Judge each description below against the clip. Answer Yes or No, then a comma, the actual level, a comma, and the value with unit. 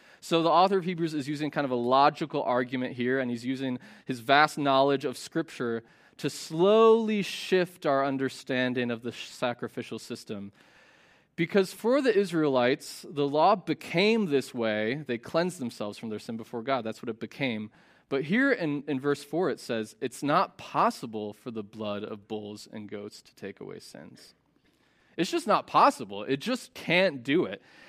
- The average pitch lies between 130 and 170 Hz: Yes, low, 135 Hz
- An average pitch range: No, wide, 5.9 semitones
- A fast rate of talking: No, average, 175 wpm